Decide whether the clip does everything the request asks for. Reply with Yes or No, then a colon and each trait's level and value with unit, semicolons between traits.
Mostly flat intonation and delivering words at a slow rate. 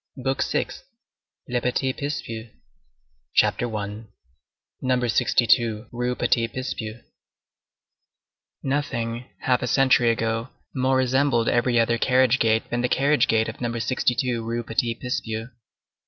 Yes: narrow, 2.1 semitones; slow, 115 wpm